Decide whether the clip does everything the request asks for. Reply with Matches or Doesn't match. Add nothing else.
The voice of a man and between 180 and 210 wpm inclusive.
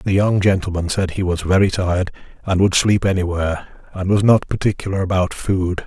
Matches